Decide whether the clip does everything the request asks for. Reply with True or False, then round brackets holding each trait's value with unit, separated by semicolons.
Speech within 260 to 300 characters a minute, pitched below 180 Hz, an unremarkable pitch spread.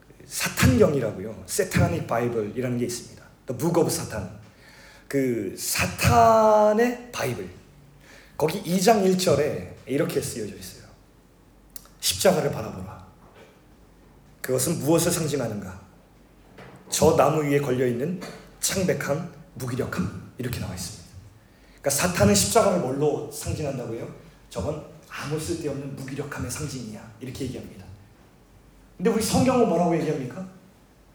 False (295 characters per minute; 140 Hz; 7.1 semitones)